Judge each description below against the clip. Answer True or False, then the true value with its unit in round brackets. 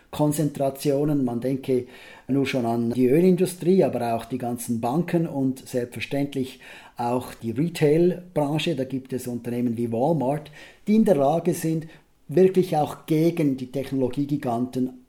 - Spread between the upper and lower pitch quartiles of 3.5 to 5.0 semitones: True (4.0 semitones)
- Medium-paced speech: True (135 wpm)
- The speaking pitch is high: False (135 Hz)